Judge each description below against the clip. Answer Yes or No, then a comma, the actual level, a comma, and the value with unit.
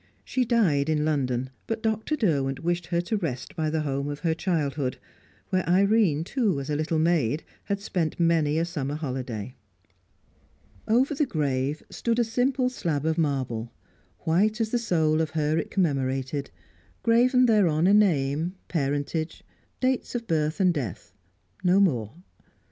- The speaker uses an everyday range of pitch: No, wide, 6.0 semitones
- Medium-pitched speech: Yes, medium, 160 Hz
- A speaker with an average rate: Yes, average, 155 wpm